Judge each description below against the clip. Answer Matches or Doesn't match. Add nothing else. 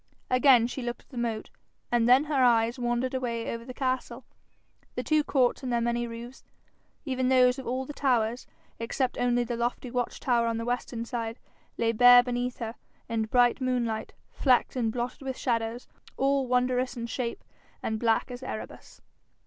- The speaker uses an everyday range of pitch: Doesn't match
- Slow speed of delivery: Doesn't match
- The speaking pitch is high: Matches